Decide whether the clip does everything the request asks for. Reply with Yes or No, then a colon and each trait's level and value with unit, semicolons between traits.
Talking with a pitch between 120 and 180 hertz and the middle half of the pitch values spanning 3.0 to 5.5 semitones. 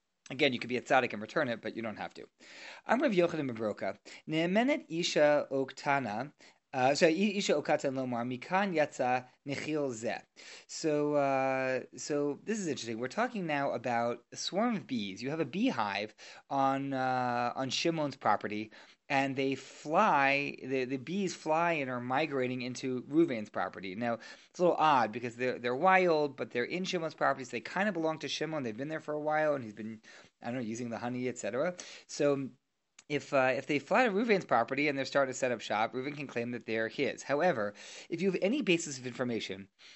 Yes: low, 135 Hz; average, 4.0 semitones